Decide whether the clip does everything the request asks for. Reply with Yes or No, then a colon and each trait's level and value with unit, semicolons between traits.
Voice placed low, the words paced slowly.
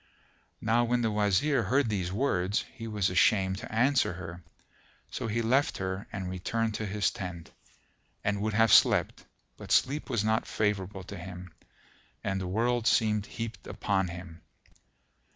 No: low, 105 Hz; average, 155 wpm